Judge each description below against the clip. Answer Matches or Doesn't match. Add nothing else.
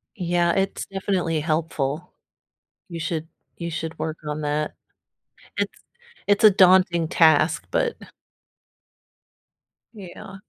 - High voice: Doesn't match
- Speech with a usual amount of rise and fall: Matches